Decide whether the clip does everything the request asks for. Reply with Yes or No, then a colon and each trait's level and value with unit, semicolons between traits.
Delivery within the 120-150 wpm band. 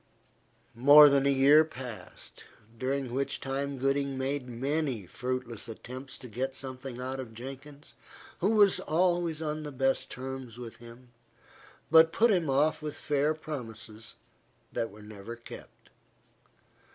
Yes: average, 140 wpm